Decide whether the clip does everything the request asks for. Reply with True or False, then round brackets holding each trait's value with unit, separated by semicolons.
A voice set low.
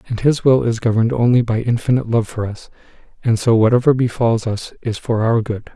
True (115 Hz)